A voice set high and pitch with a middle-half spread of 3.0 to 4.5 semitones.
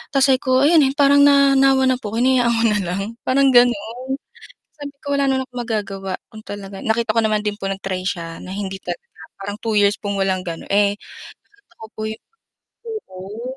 No: high, 225 Hz; average, 4.9 semitones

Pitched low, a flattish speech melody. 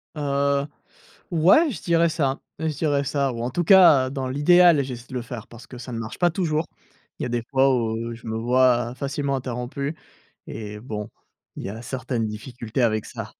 No: low, 130 Hz; average, 3.7 semitones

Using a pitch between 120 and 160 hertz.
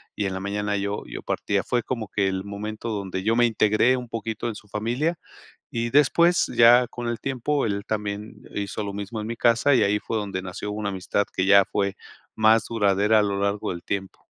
No: low, 105 Hz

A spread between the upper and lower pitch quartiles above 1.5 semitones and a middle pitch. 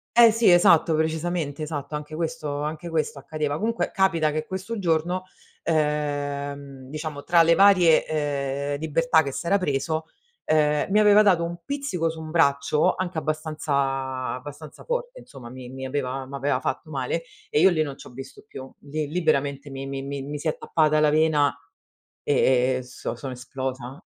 Yes: average, 2.9 semitones; medium, 150 Hz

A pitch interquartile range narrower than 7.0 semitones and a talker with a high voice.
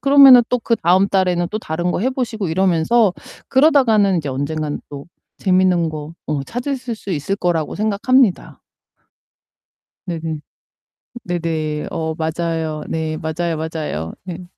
No: average, 5.2 semitones; medium, 175 Hz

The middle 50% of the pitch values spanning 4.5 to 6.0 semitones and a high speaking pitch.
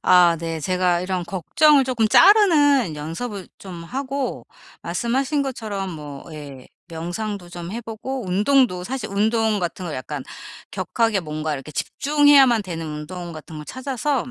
No: wide, 7.5 semitones; high, 195 Hz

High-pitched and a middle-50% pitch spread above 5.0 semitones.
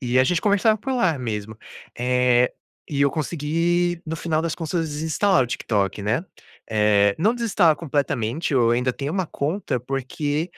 No: medium, 145 Hz; wide, 5.6 semitones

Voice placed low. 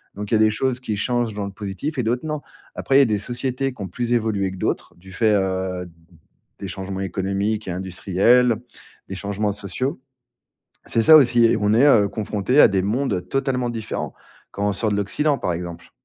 Yes: low, 105 Hz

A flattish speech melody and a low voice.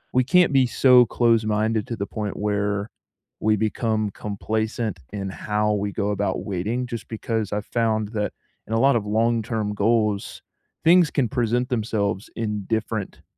Yes: narrow, 2.1 semitones; low, 110 Hz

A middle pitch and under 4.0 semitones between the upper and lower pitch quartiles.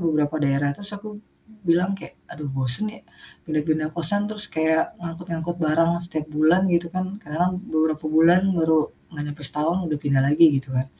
Yes: medium, 160 Hz; narrow, 2.4 semitones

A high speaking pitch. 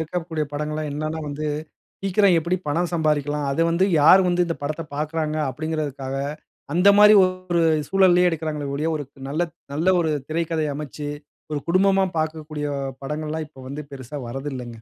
No: medium, 155 Hz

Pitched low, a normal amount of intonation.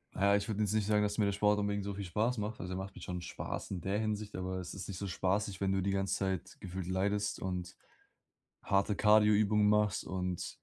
No: low, 100 Hz; narrow, 1.8 semitones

